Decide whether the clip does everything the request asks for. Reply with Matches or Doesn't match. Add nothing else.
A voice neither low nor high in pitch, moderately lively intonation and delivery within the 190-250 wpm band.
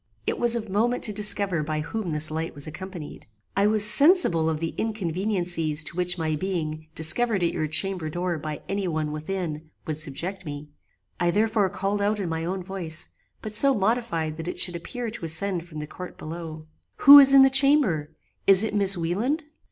Matches